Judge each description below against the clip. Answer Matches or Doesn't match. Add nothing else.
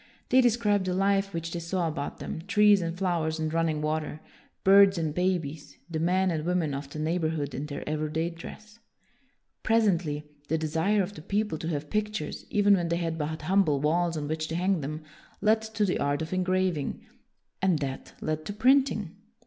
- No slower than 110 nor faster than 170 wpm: Doesn't match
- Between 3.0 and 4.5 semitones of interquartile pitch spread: Matches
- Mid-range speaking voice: Matches